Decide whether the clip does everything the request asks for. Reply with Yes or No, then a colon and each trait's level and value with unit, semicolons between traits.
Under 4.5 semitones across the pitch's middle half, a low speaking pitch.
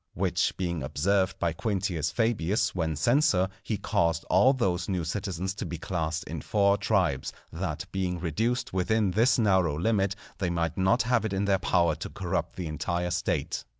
Yes: average, 3.4 semitones; very low, 95 Hz